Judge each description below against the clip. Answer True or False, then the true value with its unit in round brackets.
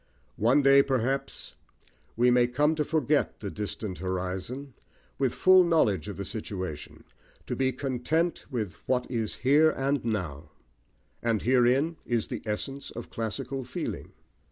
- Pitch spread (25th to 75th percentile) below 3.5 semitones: False (4.5 semitones)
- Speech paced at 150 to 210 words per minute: False (140 wpm)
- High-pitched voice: False (125 Hz)